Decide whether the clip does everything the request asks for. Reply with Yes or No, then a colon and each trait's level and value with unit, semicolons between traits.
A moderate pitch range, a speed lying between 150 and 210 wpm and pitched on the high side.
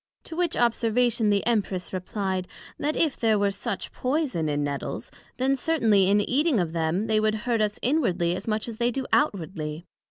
Yes: average, 4.9 semitones; average, 185 wpm; high, 215 Hz